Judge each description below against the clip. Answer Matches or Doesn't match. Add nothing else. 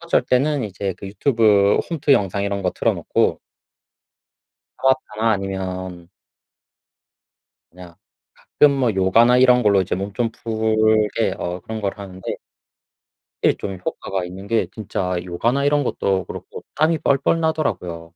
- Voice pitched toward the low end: Matches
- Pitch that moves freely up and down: Doesn't match